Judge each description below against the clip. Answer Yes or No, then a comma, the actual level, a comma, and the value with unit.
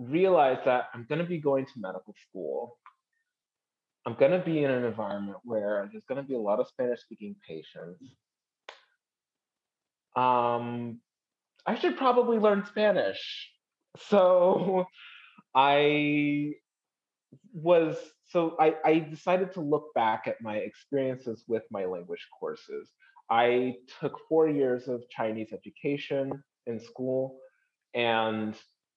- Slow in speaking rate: Yes, slow, 125 wpm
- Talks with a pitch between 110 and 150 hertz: Yes, medium, 140 Hz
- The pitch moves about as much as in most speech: No, wide, 7.3 semitones